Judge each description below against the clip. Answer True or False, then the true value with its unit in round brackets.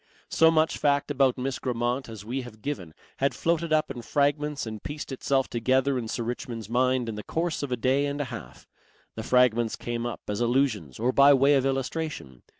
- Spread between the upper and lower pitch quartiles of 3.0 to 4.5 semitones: True (3.3 semitones)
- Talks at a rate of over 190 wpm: True (205 wpm)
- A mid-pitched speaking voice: False (130 Hz)